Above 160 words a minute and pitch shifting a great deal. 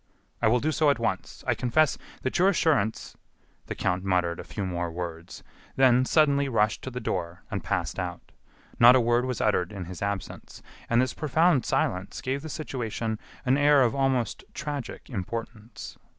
Yes: average, 180 wpm; wide, 6.2 semitones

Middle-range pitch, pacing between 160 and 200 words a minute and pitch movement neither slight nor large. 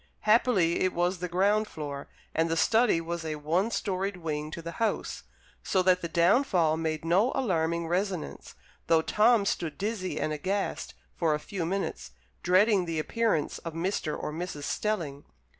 Yes: medium, 175 Hz; average, 165 wpm; average, 3.6 semitones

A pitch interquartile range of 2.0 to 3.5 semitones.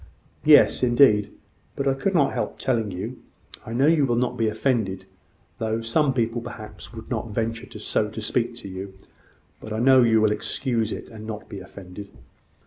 Yes: average, 2.7 semitones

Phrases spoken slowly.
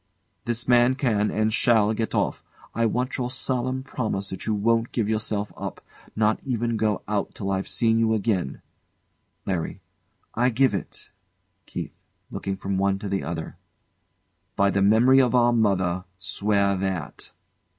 No: average, 155 wpm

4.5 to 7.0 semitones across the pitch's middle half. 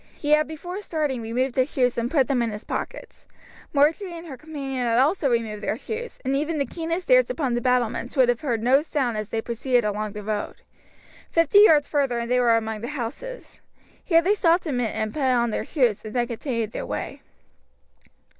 Yes: average, 4.9 semitones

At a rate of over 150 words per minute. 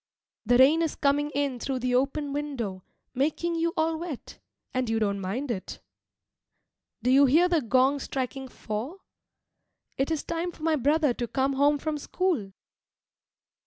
Yes: average, 160 wpm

